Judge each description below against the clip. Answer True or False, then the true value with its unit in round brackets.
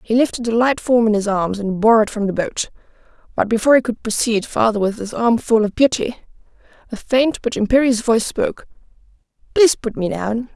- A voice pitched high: True (225 Hz)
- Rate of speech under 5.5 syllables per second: False (5.7 syllables/s)